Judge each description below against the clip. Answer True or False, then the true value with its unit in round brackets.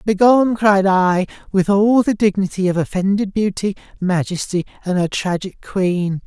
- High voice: True (195 Hz)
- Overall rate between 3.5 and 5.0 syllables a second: True (4.6 syllables/s)